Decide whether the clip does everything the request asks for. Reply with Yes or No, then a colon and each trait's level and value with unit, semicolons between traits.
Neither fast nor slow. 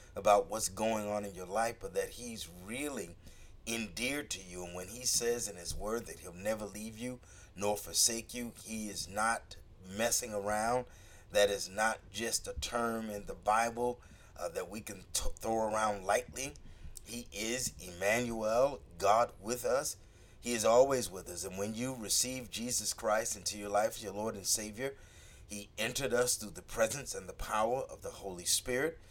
Yes: average, 185 wpm